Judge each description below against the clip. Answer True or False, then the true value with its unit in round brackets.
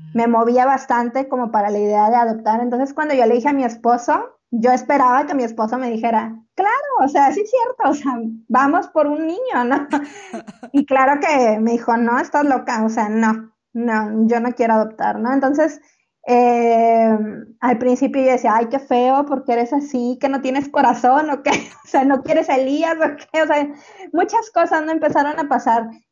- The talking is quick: True (200 wpm)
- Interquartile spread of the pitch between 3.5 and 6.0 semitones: True (3.9 semitones)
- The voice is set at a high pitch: True (255 Hz)